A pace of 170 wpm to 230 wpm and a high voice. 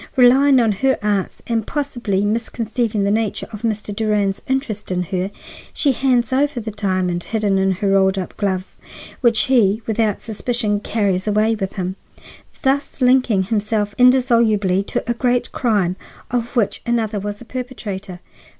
No: average, 155 wpm; high, 215 Hz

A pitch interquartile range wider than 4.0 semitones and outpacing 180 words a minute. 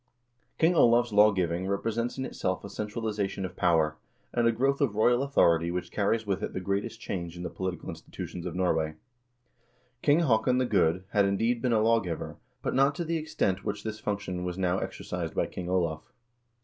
Yes: average, 4.5 semitones; average, 190 wpm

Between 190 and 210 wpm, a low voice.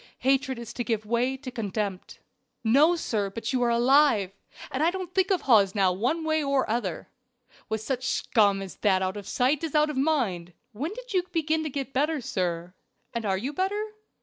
No: average, 200 wpm; very high, 255 Hz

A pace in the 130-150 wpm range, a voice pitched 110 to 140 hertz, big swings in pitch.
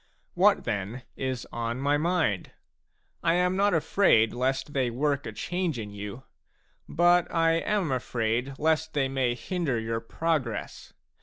Yes: average, 145 wpm; low, 135 Hz; wide, 6.0 semitones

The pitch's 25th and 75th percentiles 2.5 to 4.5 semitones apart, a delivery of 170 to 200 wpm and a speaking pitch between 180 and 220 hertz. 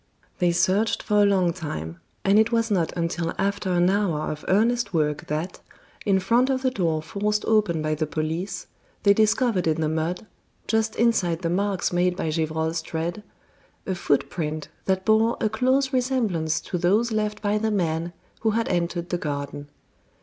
No: average, 4.9 semitones; average, 175 wpm; medium, 185 Hz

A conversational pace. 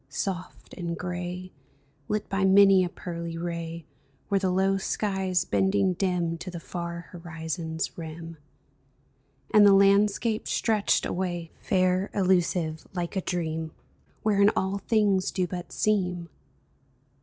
No: slow, 125 wpm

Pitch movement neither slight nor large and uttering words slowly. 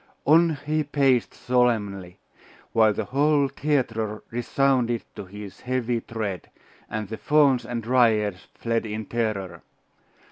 Yes: average, 3.9 semitones; slow, 120 wpm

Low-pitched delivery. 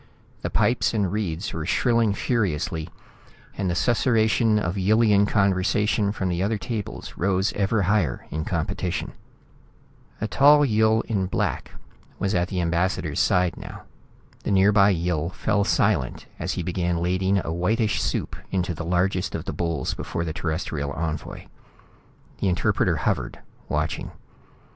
Yes: very low, 95 Hz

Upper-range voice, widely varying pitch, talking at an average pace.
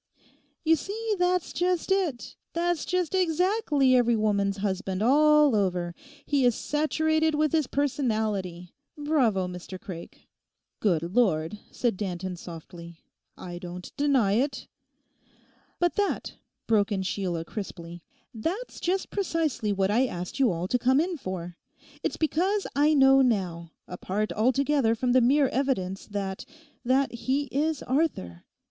No: high, 245 Hz; wide, 8.1 semitones; slow, 130 wpm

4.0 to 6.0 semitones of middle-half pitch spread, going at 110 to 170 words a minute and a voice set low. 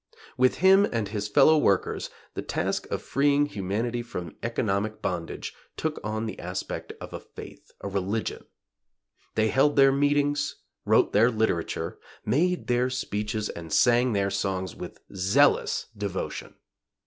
Yes: wide, 5.5 semitones; average, 140 wpm; low, 110 Hz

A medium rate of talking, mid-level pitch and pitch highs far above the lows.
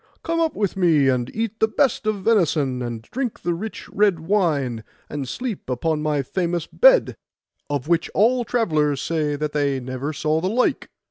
Yes: average, 180 wpm; medium, 165 Hz; wide, 7.1 semitones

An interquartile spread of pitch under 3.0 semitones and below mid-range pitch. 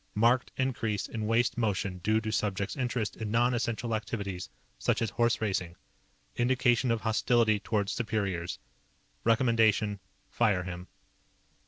Yes: narrow, 2.6 semitones; low, 110 Hz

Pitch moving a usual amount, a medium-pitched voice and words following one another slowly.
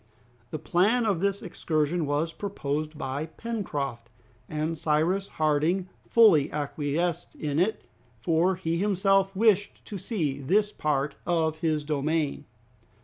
Yes: average, 4.4 semitones; medium, 160 Hz; slow, 125 wpm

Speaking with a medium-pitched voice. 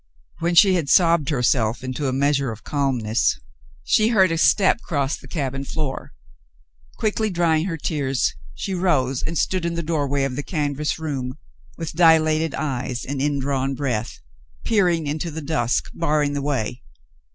Yes: medium, 145 Hz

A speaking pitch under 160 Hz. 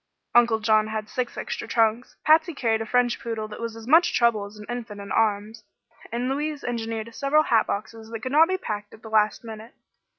No: high, 225 Hz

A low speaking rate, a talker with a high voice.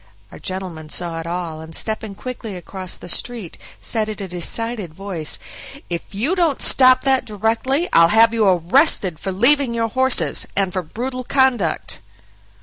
No: average, 160 wpm; high, 210 Hz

